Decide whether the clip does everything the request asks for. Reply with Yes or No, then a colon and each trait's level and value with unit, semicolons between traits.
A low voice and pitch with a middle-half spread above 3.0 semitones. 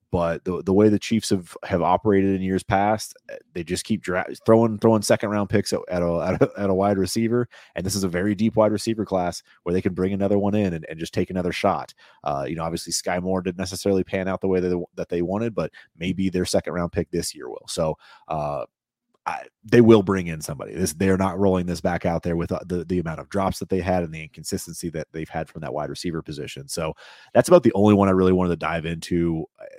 No: very low, 95 Hz; average, 2.7 semitones